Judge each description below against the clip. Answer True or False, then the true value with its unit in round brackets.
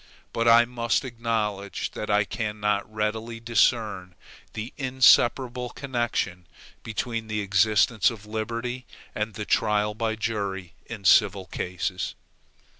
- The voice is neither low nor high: False (110 Hz)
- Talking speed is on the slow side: True (115 wpm)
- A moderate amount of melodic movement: False (2.2 semitones)